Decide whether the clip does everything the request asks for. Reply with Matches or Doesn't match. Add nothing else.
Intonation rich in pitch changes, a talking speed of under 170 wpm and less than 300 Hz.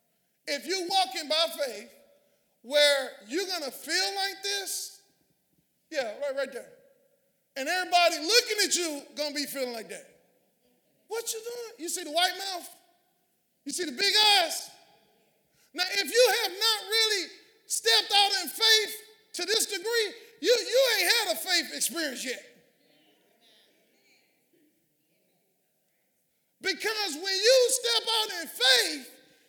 Doesn't match